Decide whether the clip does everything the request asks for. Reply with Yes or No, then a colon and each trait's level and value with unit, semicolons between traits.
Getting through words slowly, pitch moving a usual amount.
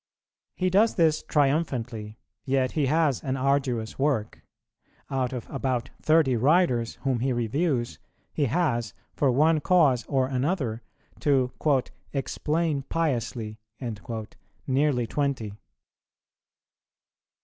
Yes: slow, 105 wpm; average, 3.9 semitones